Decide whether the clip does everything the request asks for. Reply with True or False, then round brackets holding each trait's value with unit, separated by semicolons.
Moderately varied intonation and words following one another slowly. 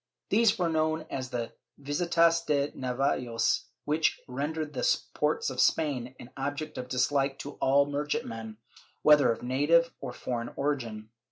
False (3.8 semitones; 150 wpm)